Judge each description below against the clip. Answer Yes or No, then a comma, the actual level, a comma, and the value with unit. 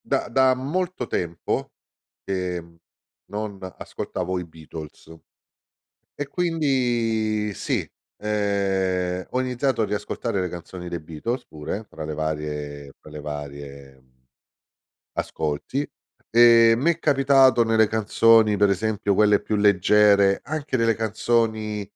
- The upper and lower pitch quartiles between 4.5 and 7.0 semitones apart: Yes, average, 5.1 semitones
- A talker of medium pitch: No, low, 105 Hz